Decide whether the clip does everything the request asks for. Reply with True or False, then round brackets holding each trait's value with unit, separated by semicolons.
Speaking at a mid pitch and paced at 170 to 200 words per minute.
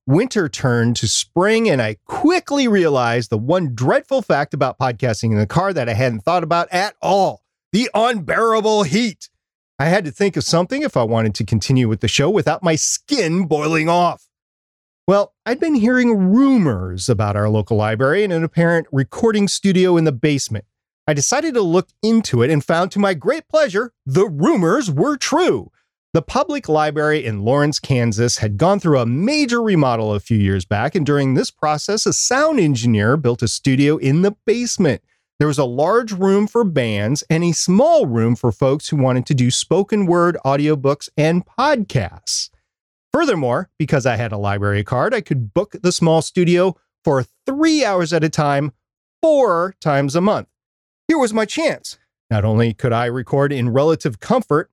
True (155 Hz; 180 wpm)